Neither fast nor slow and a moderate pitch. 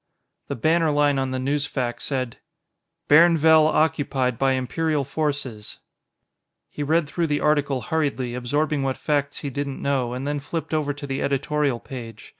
Yes: average, 155 wpm; medium, 145 Hz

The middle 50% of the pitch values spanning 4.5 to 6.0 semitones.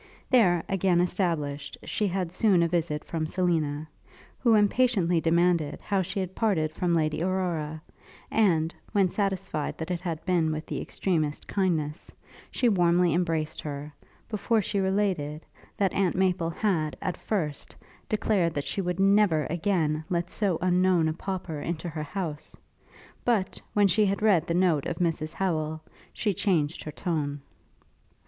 No: average, 3.5 semitones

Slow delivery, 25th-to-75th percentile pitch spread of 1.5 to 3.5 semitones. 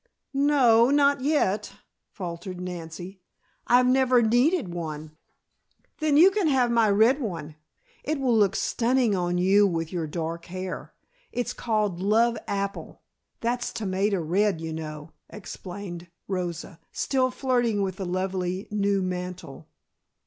No: slow, 130 wpm; wide, 5.5 semitones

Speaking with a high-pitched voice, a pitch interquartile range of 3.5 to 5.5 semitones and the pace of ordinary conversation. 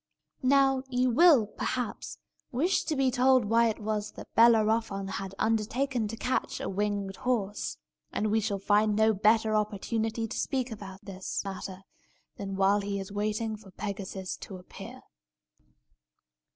No: high, 215 Hz; average, 2.9 semitones; average, 150 wpm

